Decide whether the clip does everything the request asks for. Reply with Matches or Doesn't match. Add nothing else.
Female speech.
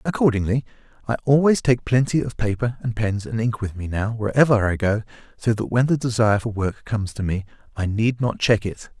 Doesn't match